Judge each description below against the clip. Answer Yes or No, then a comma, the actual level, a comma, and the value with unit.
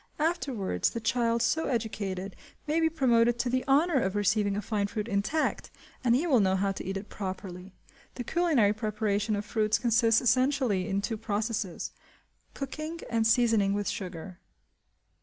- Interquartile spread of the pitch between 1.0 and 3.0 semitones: No, average, 3.9 semitones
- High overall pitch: Yes, high, 220 Hz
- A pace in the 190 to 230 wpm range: No, average, 160 wpm